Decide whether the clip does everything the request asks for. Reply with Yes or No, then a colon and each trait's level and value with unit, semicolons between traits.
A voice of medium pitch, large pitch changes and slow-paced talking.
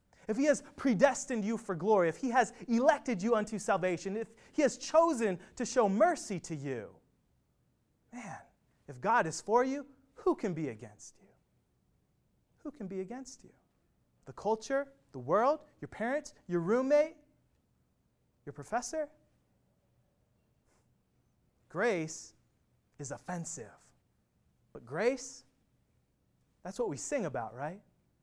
No: high, 230 Hz; wide, 7.3 semitones; slow, 130 wpm